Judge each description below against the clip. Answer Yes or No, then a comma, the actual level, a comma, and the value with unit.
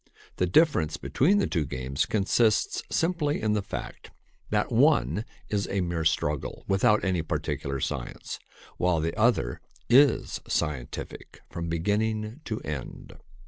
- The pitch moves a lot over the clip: Yes, wide, 5.9 semitones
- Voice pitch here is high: No, very low, 95 Hz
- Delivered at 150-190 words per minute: No, slow, 135 wpm